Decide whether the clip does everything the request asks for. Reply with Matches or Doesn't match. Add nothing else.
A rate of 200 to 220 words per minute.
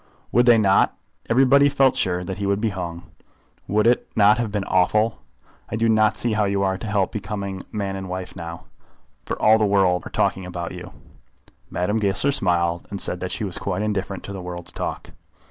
Matches